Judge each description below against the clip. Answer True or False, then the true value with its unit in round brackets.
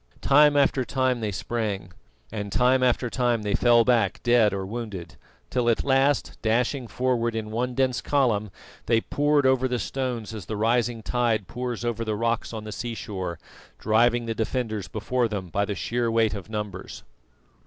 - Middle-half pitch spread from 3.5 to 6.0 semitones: False (2.7 semitones)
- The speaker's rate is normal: True (175 wpm)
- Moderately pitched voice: False (115 Hz)